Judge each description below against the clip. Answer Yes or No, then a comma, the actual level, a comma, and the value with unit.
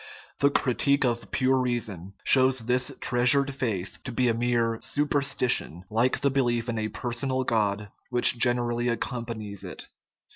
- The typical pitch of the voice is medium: No, low, 120 Hz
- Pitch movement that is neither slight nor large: No, narrow, 2.2 semitones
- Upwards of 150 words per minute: No, average, 145 wpm